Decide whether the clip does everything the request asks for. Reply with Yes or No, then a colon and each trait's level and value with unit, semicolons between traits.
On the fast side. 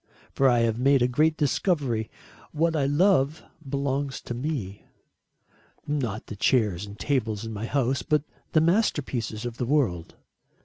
No: average, 150 wpm